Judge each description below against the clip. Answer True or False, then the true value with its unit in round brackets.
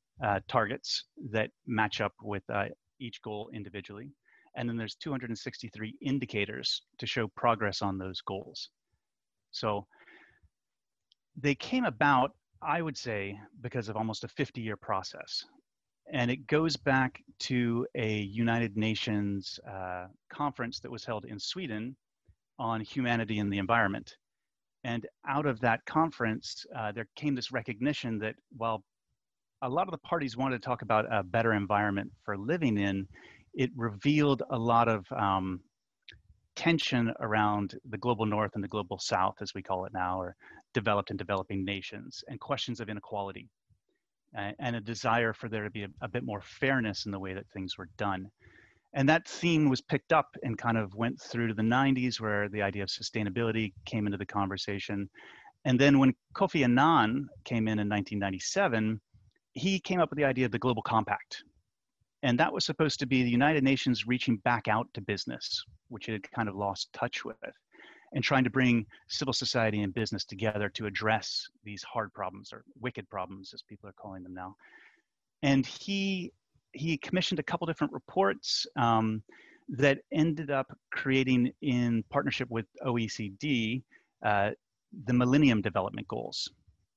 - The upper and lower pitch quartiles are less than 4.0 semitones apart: False (4.3 semitones)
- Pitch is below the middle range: True (115 Hz)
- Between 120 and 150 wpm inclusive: False (165 wpm)